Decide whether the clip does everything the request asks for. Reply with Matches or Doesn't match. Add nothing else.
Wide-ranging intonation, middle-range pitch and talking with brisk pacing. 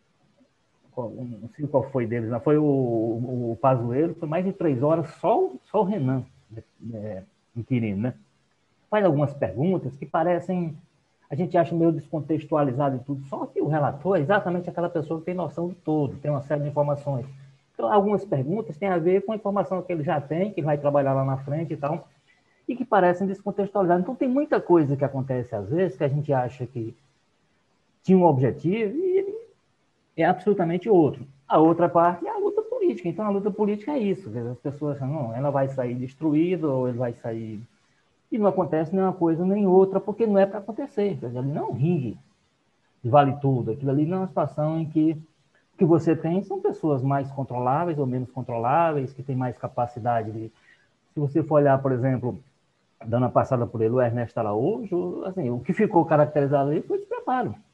Matches